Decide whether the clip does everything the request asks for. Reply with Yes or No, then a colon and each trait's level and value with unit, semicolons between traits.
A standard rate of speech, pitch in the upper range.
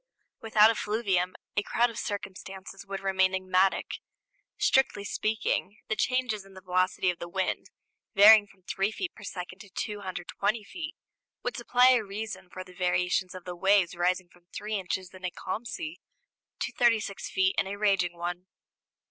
Yes: average, 165 wpm; high, 195 Hz